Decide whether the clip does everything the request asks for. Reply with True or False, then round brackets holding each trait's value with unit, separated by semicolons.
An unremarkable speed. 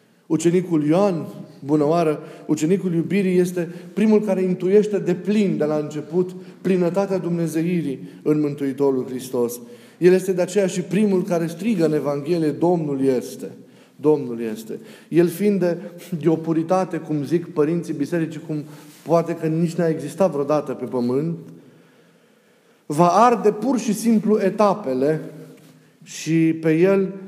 True (135 wpm)